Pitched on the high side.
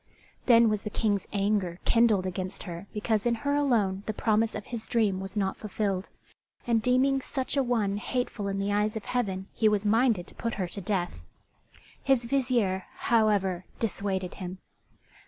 Yes: high, 210 Hz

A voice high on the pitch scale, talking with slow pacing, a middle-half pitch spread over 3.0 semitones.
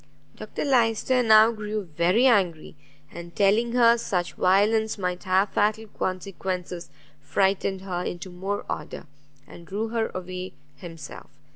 Yes: high, 195 Hz; slow, 130 wpm; average, 3.4 semitones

